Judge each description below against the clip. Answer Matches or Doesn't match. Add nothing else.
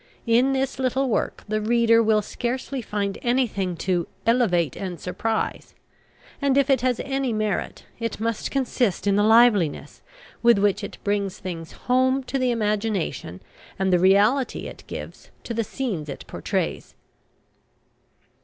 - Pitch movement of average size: Matches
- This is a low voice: Doesn't match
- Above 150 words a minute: Doesn't match